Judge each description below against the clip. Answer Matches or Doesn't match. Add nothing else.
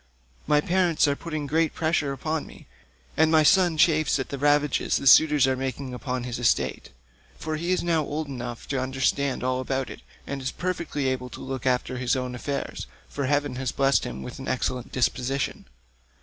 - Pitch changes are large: Doesn't match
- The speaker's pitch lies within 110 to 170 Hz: Matches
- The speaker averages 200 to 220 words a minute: Doesn't match